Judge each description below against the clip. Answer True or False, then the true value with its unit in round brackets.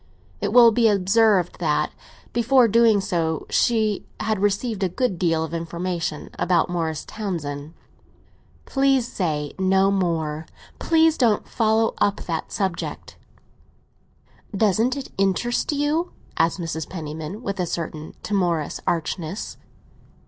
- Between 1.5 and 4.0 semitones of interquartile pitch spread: False (5.2 semitones)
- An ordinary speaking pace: False (120 wpm)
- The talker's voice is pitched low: False (190 Hz)